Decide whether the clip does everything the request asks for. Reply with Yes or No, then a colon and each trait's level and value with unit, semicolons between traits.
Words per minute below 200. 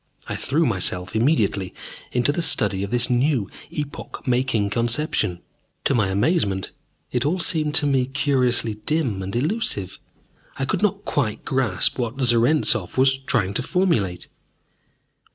Yes: average, 140 wpm